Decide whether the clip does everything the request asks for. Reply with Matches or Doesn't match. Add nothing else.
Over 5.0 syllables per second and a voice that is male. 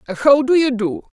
Doesn't match